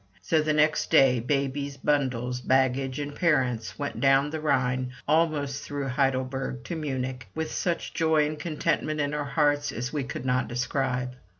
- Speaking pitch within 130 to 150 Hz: Yes, medium, 140 Hz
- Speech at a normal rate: Yes, average, 165 wpm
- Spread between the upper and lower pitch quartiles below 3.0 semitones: Yes, narrow, 2.6 semitones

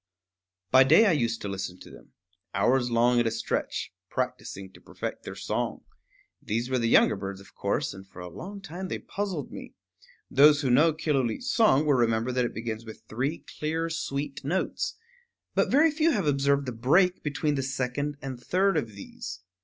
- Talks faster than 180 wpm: Yes, average, 190 wpm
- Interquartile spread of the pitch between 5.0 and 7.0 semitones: Yes, wide, 5.6 semitones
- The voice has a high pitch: No, low, 135 Hz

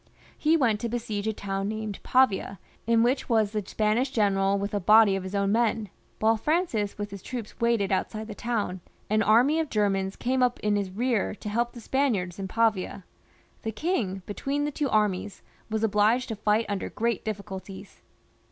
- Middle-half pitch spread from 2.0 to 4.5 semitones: Yes, average, 2.8 semitones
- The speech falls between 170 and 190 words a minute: Yes, average, 180 wpm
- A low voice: No, high, 215 Hz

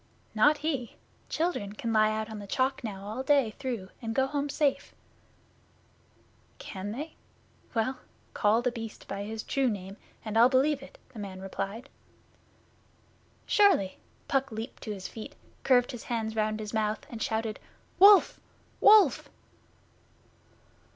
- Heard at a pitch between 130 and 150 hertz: No, high, 225 Hz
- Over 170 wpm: No, average, 145 wpm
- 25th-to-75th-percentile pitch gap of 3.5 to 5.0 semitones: Yes, average, 4.0 semitones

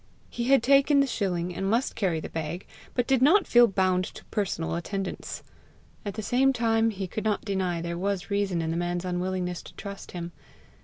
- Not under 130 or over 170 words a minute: No, average, 200 wpm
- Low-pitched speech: No, high, 195 Hz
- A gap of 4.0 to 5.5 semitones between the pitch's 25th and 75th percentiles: Yes, average, 4.4 semitones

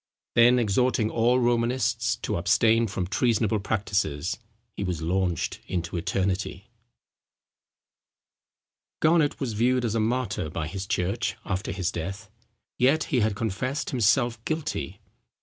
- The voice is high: No, low, 110 Hz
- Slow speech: Yes, slow, 125 wpm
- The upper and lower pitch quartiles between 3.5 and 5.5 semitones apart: Yes, average, 4.3 semitones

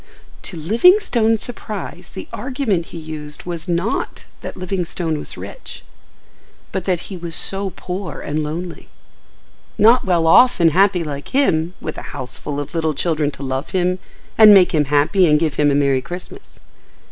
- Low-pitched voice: No, medium, 170 Hz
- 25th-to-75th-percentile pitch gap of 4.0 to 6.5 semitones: Yes, average, 4.3 semitones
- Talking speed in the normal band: Yes, average, 170 wpm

